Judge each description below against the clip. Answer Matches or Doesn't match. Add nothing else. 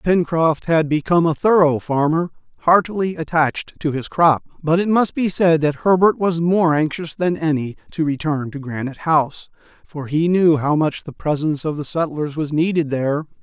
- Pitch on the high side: Doesn't match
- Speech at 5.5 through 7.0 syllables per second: Doesn't match